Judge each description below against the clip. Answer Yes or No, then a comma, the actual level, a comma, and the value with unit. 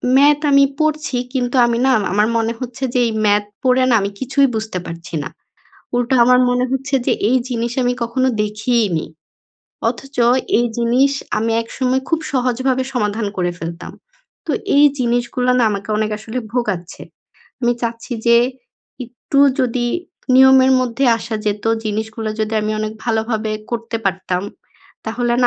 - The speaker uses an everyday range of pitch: Yes, average, 3.1 semitones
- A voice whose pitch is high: Yes, high, 240 Hz